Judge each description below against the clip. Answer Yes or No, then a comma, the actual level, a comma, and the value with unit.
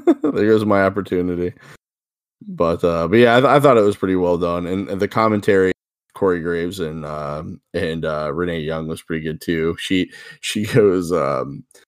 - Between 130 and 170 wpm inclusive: No, average, 180 wpm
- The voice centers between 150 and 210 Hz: No, very low, 90 Hz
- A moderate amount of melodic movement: Yes, average, 3.7 semitones